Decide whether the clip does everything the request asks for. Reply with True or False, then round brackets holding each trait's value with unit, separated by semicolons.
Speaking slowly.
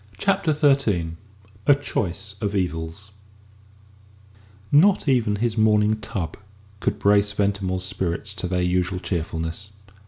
True (115 wpm)